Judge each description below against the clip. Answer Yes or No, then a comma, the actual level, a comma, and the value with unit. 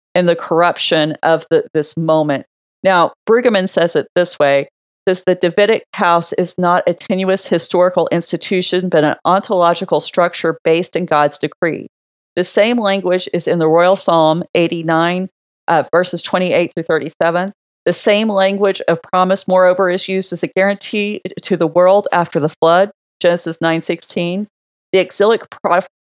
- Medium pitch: Yes, medium, 175 Hz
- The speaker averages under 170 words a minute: Yes, average, 155 wpm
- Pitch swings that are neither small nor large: No, narrow, 2.3 semitones